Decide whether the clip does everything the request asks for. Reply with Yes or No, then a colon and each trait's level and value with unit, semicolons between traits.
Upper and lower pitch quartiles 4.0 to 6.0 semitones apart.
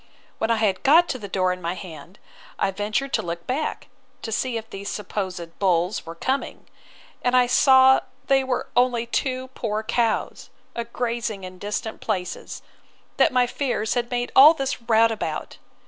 Yes: average, 4.7 semitones